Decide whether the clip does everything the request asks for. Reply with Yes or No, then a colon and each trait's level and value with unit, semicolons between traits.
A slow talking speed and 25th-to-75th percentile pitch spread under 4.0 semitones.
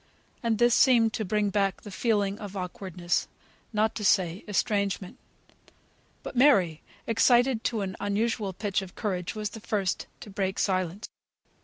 No: average, 150 wpm; average, 2.7 semitones